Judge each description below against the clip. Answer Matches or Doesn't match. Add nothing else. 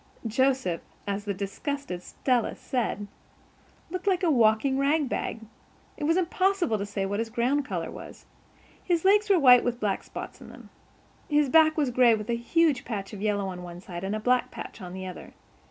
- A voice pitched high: Matches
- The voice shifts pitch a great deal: Matches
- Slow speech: Doesn't match